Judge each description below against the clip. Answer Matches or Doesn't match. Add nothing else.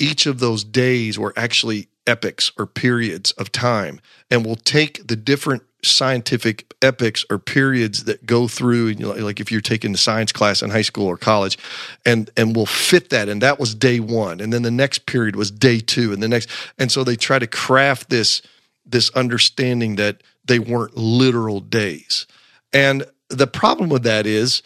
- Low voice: Matches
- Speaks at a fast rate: Doesn't match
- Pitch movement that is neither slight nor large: Matches